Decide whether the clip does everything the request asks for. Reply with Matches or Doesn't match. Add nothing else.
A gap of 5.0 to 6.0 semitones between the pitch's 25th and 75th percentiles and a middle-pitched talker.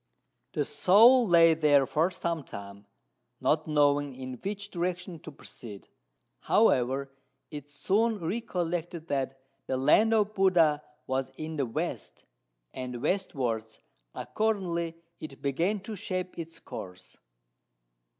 Matches